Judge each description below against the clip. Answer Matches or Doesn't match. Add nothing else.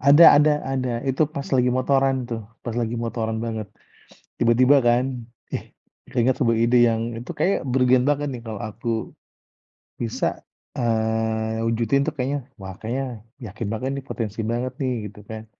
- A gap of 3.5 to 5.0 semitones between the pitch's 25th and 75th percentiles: Doesn't match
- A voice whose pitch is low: Matches